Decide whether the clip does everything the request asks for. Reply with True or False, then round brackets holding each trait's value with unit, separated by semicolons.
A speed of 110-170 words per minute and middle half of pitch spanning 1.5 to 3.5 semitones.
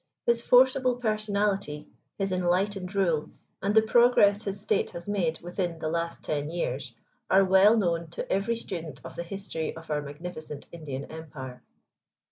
False (155 wpm; 4.2 semitones)